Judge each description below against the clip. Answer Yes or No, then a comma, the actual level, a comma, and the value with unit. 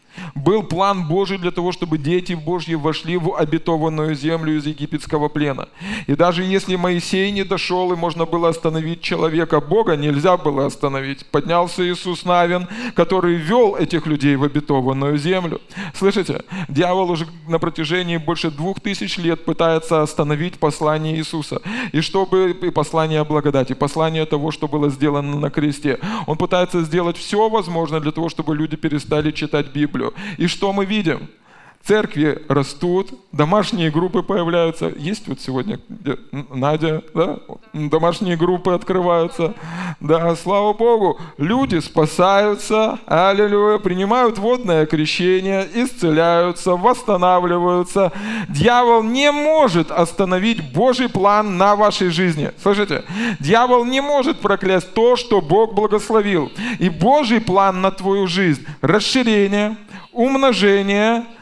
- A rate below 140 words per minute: Yes, average, 130 wpm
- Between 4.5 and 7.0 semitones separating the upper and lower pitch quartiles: No, average, 3.9 semitones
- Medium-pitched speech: Yes, medium, 175 Hz